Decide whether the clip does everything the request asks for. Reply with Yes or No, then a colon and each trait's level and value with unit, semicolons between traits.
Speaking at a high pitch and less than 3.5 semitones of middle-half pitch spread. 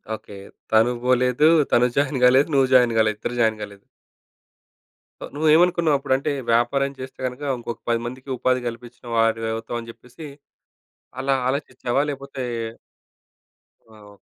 No: low, 125 Hz; average, 2.9 semitones